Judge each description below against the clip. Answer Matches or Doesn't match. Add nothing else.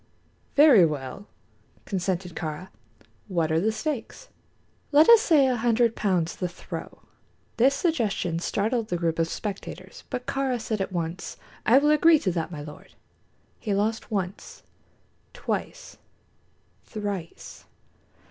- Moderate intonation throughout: Doesn't match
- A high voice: Matches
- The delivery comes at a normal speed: Doesn't match